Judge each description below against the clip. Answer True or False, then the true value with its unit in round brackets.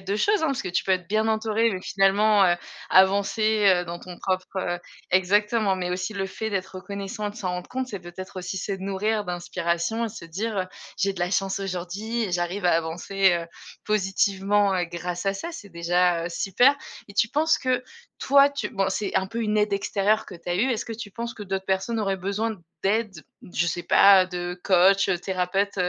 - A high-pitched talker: True (195 Hz)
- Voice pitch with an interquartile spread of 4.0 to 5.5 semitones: False (2.9 semitones)